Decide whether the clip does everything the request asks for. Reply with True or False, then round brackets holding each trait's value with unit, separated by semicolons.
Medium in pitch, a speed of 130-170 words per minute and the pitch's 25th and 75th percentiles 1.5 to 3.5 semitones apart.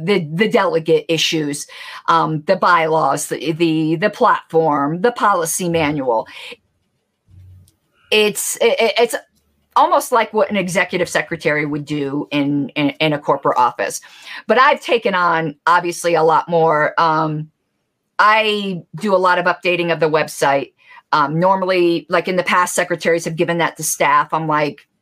True (165 Hz; 150 wpm; 3.2 semitones)